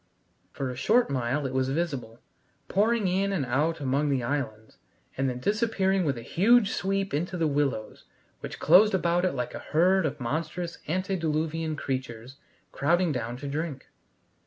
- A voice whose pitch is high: No, medium, 155 Hz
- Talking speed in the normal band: Yes, average, 160 wpm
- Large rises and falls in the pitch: Yes, wide, 5.8 semitones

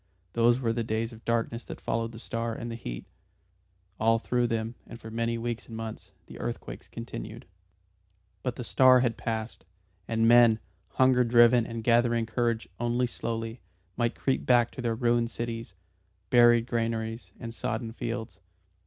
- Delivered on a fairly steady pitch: Yes, narrow, 1.0 semitones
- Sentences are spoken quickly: No, average, 160 wpm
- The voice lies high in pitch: No, low, 115 Hz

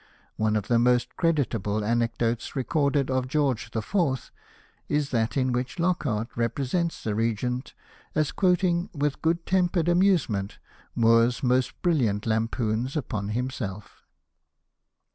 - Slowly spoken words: Yes, slow, 120 wpm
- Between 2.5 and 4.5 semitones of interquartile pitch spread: No, average, 5.1 semitones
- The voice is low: Yes, low, 125 Hz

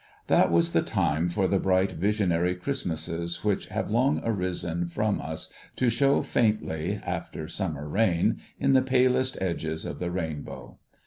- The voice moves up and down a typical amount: Yes, average, 4.5 semitones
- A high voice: No, very low, 90 Hz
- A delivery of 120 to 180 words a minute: Yes, average, 150 wpm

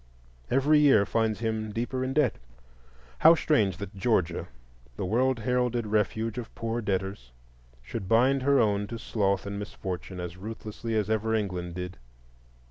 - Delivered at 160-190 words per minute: No, average, 150 wpm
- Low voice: Yes, low, 110 Hz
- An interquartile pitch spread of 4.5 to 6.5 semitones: No, average, 3.6 semitones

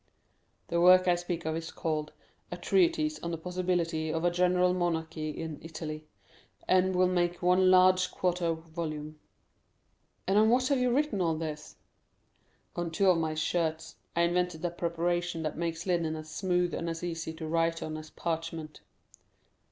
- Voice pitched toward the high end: No, medium, 170 Hz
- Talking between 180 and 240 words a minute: No, average, 165 wpm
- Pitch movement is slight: Yes, narrow, 2.0 semitones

